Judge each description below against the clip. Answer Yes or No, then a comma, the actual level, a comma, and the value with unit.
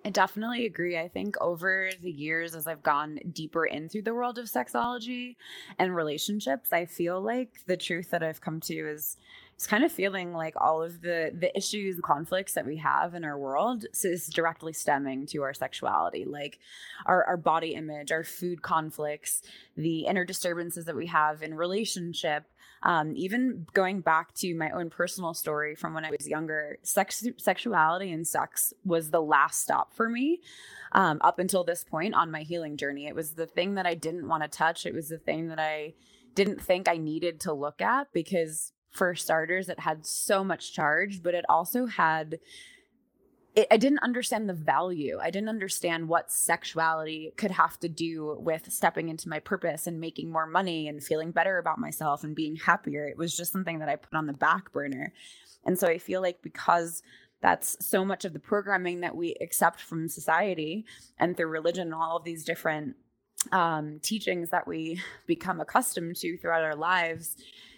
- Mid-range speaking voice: Yes, medium, 170 Hz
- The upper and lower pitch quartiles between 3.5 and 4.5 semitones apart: No, average, 3.0 semitones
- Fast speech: No, average, 190 wpm